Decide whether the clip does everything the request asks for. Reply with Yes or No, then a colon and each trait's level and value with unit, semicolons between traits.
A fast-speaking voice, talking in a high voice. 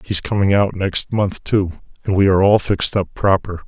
No: fast, 210 wpm; very low, 95 Hz